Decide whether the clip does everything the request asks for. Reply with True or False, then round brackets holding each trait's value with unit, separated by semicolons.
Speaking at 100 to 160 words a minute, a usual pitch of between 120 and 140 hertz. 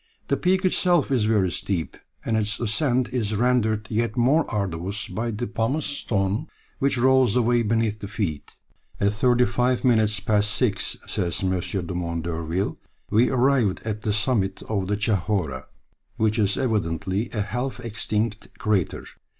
False (150 wpm; 110 Hz)